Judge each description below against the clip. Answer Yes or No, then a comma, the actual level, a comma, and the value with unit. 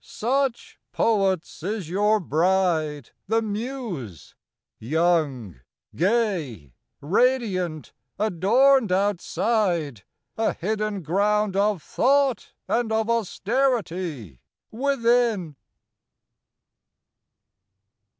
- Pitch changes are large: Yes, wide, 5.8 semitones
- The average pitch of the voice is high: Yes, high, 200 Hz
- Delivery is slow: Yes, slow, 70 wpm